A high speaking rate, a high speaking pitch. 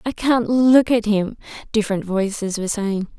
No: average, 170 wpm; high, 215 Hz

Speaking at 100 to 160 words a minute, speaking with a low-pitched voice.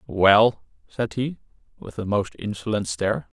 Yes: average, 140 wpm; low, 100 Hz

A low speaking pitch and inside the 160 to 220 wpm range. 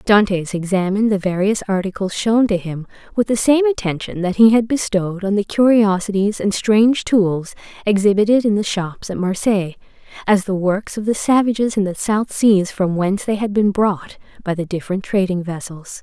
No: high, 200 Hz; average, 185 wpm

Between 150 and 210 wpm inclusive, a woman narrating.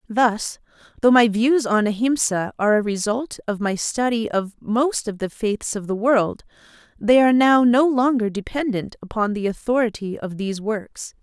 Yes: average, 170 wpm; female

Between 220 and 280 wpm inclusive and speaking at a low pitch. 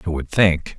Yes: fast, 230 wpm; very low, 85 Hz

